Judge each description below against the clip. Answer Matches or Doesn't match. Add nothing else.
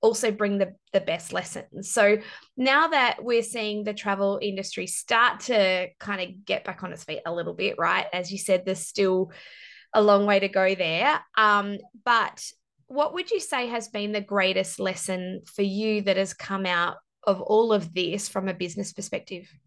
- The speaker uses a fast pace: Doesn't match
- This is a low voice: Doesn't match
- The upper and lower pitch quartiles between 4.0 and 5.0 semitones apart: Doesn't match